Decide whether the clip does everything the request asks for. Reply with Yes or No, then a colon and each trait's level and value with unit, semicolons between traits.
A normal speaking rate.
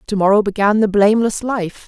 Yes: average, 190 wpm